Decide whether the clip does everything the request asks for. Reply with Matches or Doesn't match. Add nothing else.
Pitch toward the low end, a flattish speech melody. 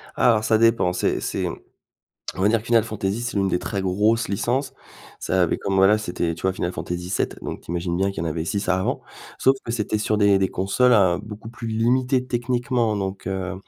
Doesn't match